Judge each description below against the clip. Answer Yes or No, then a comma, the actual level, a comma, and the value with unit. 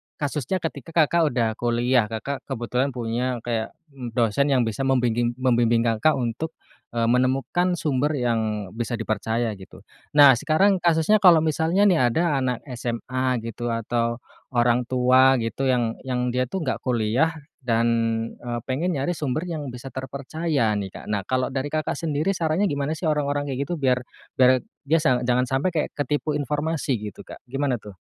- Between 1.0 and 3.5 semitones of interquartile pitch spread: No, average, 4.0 semitones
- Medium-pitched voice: No, low, 130 Hz